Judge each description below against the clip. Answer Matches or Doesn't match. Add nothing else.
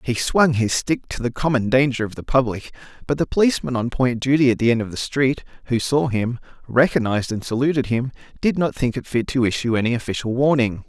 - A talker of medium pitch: Doesn't match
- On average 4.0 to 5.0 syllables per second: Doesn't match